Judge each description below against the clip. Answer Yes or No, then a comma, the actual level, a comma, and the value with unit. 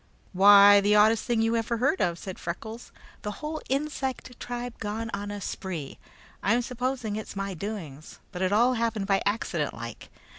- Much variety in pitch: No, average, 3.4 semitones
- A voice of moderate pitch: No, high, 210 Hz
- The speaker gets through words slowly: No, average, 175 wpm